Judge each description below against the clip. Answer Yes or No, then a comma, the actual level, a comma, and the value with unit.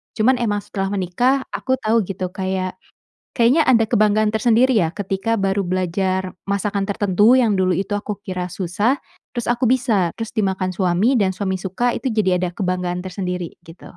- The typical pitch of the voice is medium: No, high, 200 Hz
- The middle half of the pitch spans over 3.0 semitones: Yes, average, 3.4 semitones